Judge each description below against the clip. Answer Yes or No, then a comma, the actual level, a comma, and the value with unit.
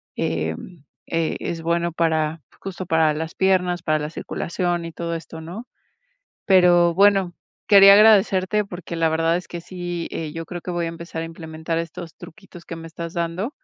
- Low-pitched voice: No, medium, 170 Hz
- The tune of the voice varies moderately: No, narrow, 1.8 semitones